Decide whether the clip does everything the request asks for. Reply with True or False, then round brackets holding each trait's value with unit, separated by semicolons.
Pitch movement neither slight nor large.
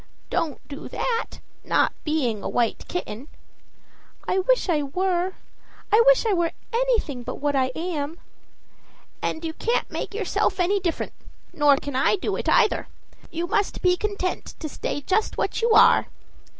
False (5.9 semitones)